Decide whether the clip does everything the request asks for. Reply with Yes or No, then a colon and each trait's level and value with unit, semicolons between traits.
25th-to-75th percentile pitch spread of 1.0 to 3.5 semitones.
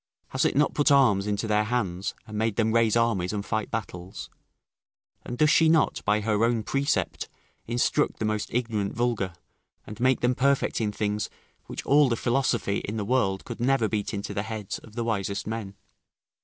Yes: average, 2.9 semitones